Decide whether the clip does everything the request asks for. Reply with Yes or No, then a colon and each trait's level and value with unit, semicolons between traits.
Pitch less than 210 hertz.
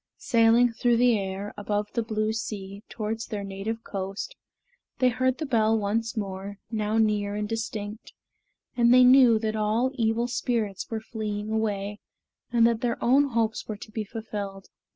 No: high, 220 Hz